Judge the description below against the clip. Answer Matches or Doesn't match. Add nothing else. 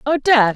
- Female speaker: Matches